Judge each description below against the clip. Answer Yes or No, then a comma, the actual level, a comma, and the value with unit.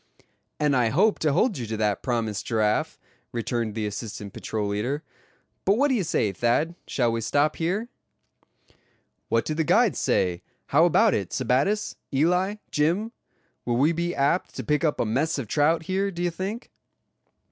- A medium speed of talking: Yes, average, 170 wpm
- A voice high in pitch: No, medium, 145 Hz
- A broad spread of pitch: Yes, wide, 7.3 semitones